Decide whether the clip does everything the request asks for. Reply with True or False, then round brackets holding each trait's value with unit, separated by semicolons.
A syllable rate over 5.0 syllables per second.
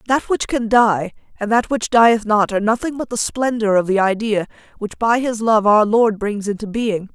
False (4.9 syllables/s)